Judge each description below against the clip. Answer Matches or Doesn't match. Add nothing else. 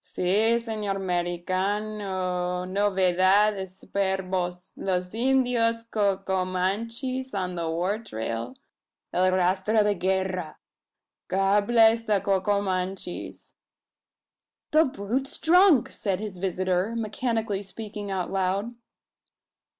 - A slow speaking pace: Matches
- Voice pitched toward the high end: Matches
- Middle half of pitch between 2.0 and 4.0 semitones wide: Matches